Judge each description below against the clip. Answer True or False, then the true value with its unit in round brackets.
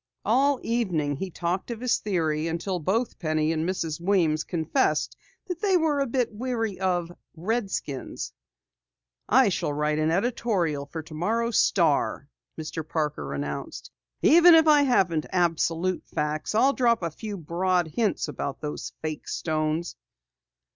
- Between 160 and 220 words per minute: False (140 wpm)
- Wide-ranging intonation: True (6.8 semitones)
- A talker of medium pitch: True (180 Hz)